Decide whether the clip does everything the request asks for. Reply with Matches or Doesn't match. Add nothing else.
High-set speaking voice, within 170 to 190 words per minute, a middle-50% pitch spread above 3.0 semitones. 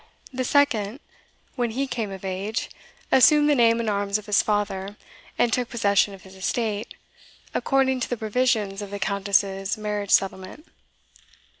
Doesn't match